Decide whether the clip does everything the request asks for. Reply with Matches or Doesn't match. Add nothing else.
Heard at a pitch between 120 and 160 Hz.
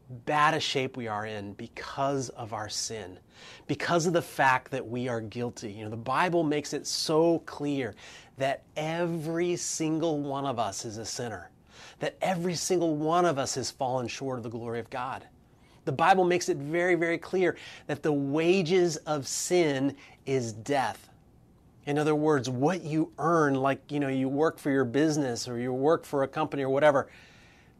Matches